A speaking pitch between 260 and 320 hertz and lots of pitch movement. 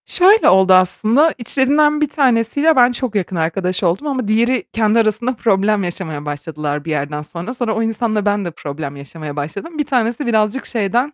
No: high, 215 Hz; wide, 6.6 semitones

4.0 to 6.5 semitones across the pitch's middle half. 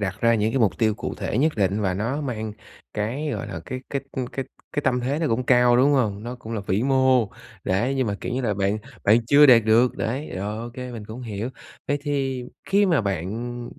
No: average, 3.6 semitones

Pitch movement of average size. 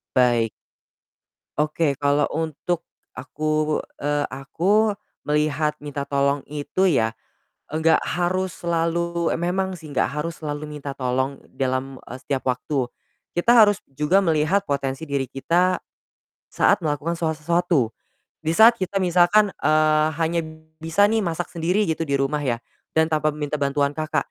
Yes: average, 3.4 semitones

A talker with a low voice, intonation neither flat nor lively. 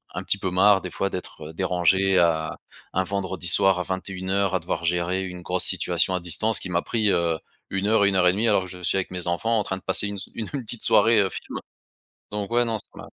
No: very low, 95 Hz; narrow, 2.1 semitones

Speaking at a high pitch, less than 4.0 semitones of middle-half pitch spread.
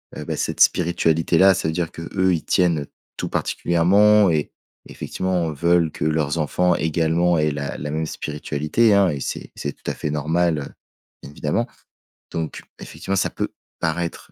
No: very low, 80 Hz; average, 2.7 semitones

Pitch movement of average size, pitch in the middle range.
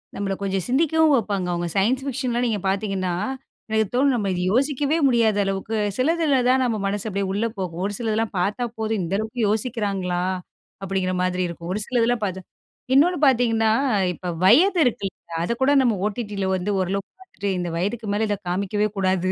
No: average, 4.2 semitones; high, 210 Hz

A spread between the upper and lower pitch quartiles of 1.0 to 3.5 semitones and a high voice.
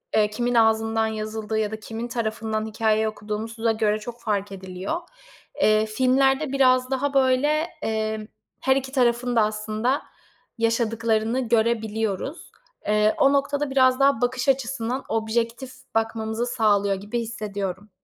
Yes: average, 2.8 semitones; high, 225 Hz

